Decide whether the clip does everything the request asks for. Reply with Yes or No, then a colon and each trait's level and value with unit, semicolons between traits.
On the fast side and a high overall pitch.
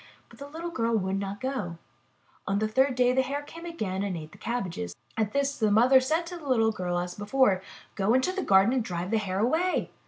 Yes: fast, 225 wpm; high, 225 Hz